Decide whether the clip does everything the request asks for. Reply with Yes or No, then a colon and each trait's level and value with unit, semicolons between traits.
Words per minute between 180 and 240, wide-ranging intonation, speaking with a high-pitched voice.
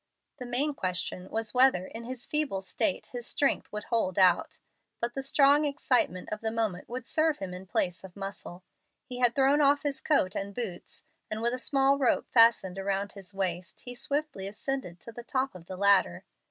Yes: average, 195 wpm; wide, 5.8 semitones; high, 230 Hz